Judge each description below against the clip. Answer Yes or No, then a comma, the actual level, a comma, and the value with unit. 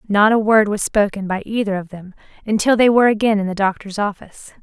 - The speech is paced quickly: Yes, fast, 220 wpm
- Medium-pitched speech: No, high, 205 Hz